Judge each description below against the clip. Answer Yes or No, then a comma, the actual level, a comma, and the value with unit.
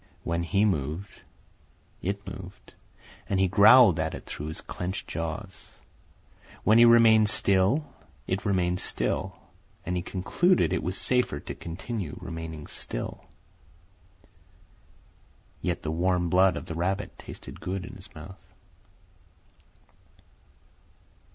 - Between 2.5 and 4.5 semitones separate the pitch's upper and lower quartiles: Yes, average, 3.2 semitones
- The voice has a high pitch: No, very low, 95 Hz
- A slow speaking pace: Yes, slow, 120 wpm